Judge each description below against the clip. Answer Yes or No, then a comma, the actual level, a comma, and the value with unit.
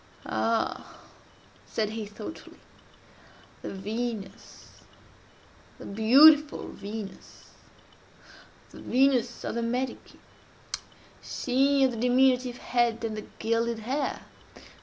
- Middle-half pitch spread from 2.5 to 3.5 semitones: Yes, average, 2.8 semitones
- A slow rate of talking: Yes, slow, 80 wpm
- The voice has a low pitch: No, high, 235 Hz